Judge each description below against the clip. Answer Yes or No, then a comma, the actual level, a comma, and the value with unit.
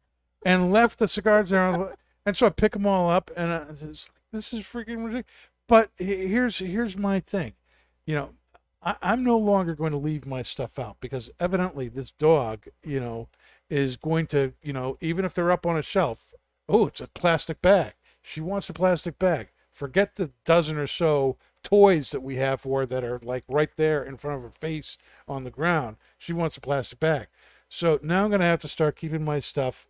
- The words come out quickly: Yes, fast, 210 wpm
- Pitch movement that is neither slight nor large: No, wide, 5.8 semitones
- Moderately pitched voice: Yes, medium, 160 Hz